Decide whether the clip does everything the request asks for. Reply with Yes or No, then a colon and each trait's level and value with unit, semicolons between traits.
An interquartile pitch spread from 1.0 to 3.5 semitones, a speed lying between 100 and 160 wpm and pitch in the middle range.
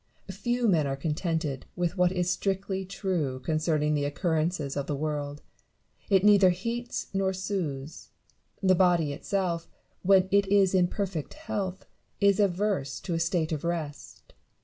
No: average, 4.0 semitones; average, 150 wpm; medium, 180 Hz